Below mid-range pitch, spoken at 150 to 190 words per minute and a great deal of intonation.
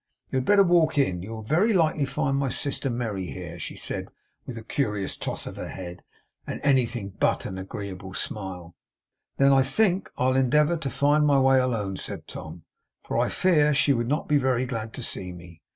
No: low, 130 Hz; average, 200 wpm; wide, 6.8 semitones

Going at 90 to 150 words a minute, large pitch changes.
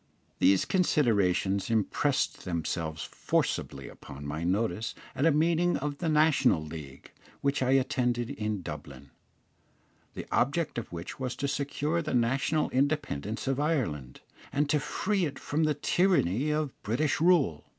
Yes: average, 140 wpm; wide, 7.7 semitones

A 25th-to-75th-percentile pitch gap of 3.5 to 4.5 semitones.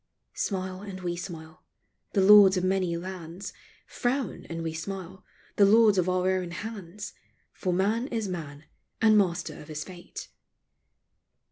No: average, 2.7 semitones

